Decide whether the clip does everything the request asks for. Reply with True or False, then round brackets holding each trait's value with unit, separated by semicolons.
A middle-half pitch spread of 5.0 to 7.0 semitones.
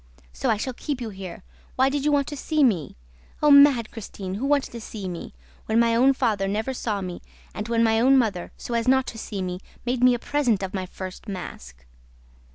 True (5.3 semitones)